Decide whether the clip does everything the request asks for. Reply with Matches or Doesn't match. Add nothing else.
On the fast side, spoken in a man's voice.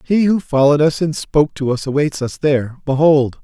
Matches